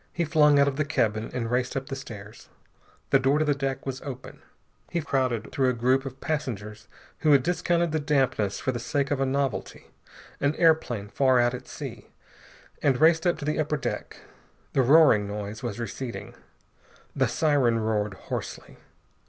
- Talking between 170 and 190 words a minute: Yes, average, 180 wpm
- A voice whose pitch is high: No, low, 135 Hz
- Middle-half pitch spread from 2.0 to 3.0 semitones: No, average, 4.0 semitones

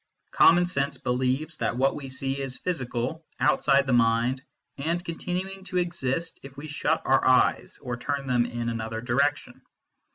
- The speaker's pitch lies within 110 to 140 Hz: Yes, low, 135 Hz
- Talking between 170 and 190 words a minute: No, average, 160 wpm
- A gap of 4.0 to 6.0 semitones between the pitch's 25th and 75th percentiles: Yes, average, 4.6 semitones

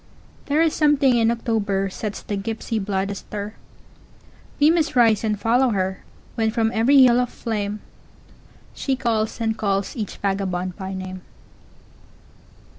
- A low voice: No, high, 220 Hz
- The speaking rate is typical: No, slow, 125 wpm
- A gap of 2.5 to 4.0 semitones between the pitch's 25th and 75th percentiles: Yes, average, 3.4 semitones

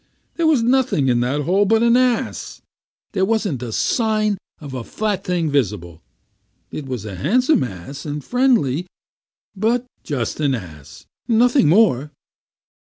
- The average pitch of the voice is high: No, medium, 175 Hz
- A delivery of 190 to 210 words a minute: No, average, 150 wpm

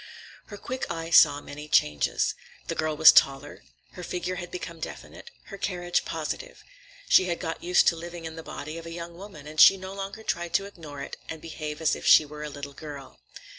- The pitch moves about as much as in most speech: Yes, average, 3.0 semitones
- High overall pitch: No, medium, 165 Hz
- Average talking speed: No, fast, 210 wpm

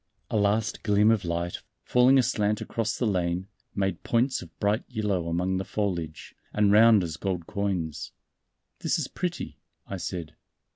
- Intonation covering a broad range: No, average, 3.7 semitones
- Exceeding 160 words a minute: No, average, 155 wpm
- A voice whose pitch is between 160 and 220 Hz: No, low, 100 Hz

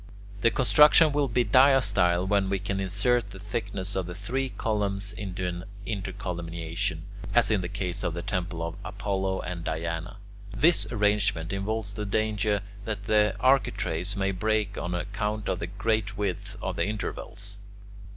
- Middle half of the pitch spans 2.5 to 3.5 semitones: Yes, average, 2.8 semitones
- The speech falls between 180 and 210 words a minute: No, average, 155 wpm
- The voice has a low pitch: Yes, low, 100 Hz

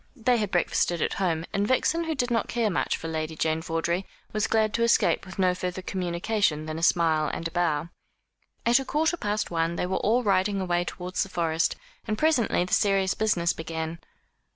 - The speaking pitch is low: No, medium, 185 Hz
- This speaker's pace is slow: No, average, 200 wpm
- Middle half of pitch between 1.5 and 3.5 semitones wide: No, average, 4.6 semitones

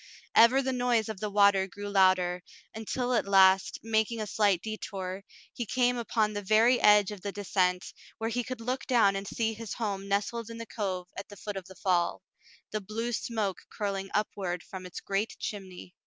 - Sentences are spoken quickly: No, average, 195 wpm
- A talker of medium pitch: No, high, 205 Hz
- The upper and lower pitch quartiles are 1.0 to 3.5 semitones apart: Yes, average, 2.8 semitones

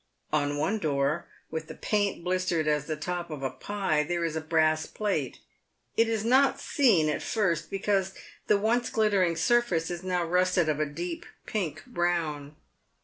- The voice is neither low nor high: Yes, medium, 175 Hz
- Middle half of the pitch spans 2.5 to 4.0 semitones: No, average, 4.5 semitones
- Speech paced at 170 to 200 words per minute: Yes, average, 175 wpm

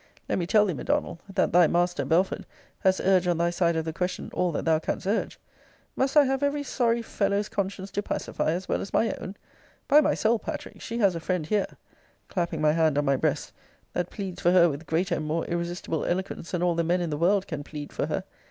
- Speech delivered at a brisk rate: Yes, fast, 235 wpm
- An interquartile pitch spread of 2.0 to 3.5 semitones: Yes, average, 3.2 semitones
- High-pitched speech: No, medium, 180 Hz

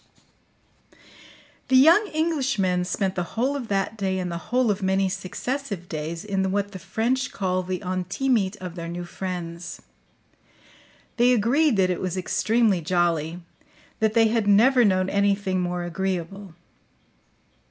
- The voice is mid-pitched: No, high, 195 Hz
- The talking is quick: No, average, 140 wpm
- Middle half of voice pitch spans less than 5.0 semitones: Yes, average, 4.0 semitones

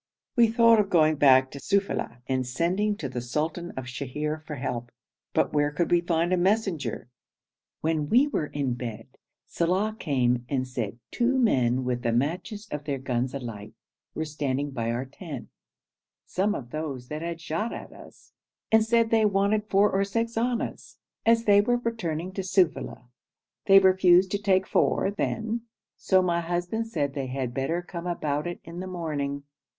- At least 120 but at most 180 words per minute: Yes, average, 175 wpm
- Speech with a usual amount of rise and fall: No, wide, 6.8 semitones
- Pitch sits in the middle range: Yes, medium, 165 Hz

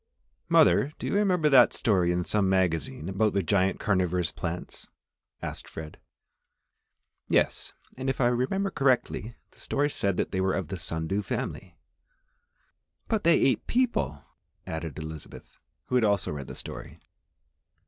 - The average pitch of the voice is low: Yes, low, 100 Hz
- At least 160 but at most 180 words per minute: No, average, 150 wpm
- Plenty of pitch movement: Yes, wide, 7.0 semitones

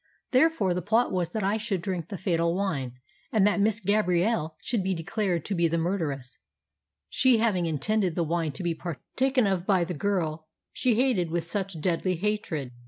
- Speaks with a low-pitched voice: No, medium, 185 Hz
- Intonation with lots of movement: No, average, 3.9 semitones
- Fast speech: No, average, 185 wpm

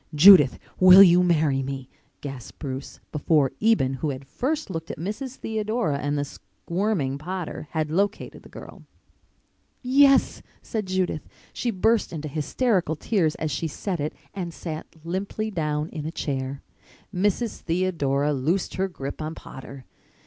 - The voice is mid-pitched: Yes, medium, 165 Hz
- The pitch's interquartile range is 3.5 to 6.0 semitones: Yes, wide, 5.4 semitones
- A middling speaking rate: Yes, average, 150 wpm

